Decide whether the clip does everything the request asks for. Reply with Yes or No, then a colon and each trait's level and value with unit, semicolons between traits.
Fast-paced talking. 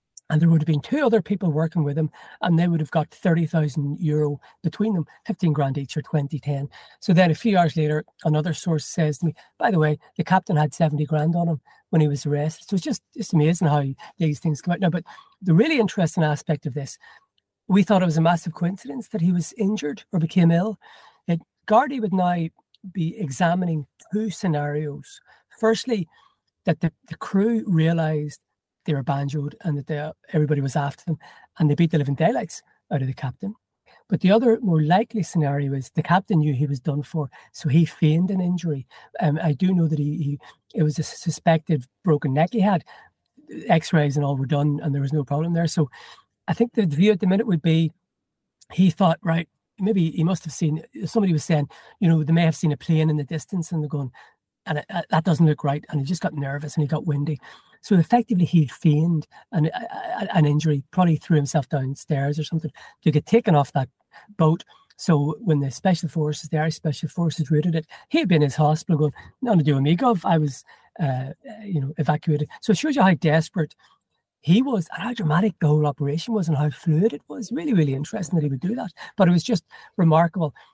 Yes: fast, 220 wpm